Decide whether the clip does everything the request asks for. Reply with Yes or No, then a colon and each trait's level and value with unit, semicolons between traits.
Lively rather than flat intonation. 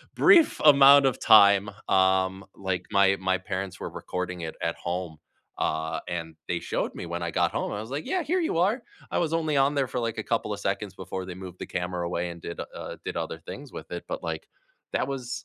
Yes: wide, 6.9 semitones